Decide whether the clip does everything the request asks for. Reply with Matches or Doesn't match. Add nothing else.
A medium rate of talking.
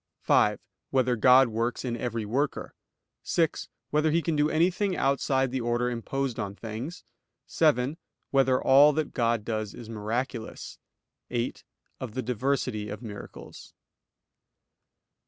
Doesn't match